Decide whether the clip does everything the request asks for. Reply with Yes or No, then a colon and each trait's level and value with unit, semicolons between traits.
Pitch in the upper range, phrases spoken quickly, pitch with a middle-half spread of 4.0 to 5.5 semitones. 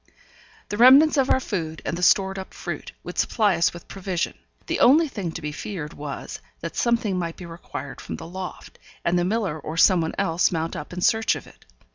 No: medium, 180 Hz; fast, 210 wpm; average, 4.3 semitones